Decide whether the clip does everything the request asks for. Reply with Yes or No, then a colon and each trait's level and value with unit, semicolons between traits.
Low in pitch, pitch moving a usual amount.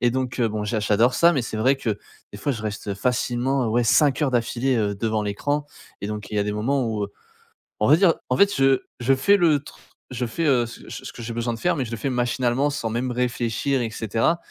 Yes: low, 120 Hz; average, 3.5 semitones